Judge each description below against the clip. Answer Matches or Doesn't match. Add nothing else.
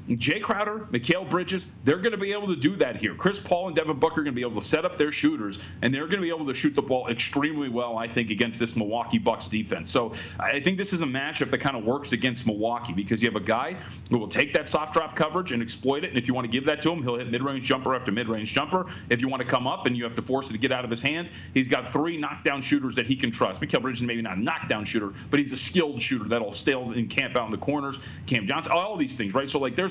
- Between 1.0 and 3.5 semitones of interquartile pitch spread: Doesn't match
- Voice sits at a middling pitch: Doesn't match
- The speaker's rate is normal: Doesn't match